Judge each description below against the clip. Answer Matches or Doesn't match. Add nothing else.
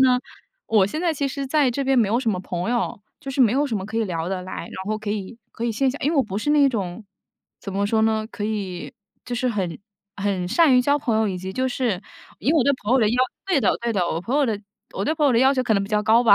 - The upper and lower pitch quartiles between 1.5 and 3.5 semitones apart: Doesn't match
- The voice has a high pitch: Matches